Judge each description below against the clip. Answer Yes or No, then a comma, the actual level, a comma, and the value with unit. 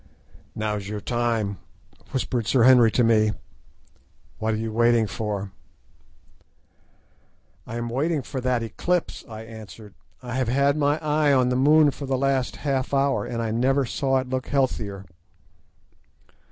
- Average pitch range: Yes, average, 3.4 semitones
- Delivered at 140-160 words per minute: Yes, average, 150 wpm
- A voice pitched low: Yes, low, 125 Hz